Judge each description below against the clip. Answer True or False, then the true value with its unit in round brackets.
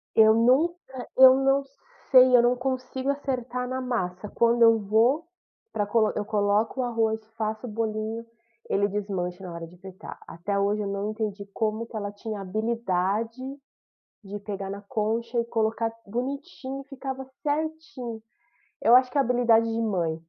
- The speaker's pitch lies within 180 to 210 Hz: False (225 Hz)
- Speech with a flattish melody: False (3.6 semitones)